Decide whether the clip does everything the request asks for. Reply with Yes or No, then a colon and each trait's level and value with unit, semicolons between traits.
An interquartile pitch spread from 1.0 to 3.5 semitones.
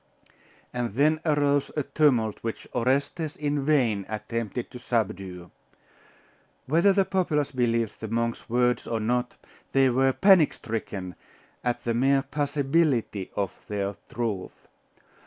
No: average, 4.5 semitones